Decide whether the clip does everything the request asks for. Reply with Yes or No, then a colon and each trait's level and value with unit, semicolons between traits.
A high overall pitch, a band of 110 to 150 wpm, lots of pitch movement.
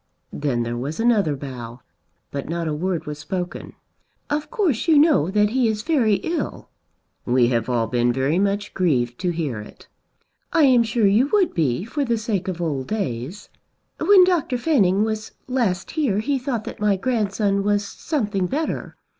No: high, 200 Hz; average, 175 wpm; wide, 8.5 semitones